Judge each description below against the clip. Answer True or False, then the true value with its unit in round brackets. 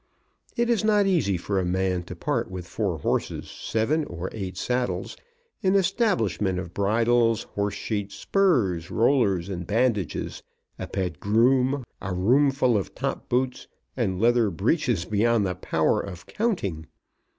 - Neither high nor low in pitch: False (105 Hz)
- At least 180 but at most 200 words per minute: False (140 wpm)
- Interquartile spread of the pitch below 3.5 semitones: False (5.4 semitones)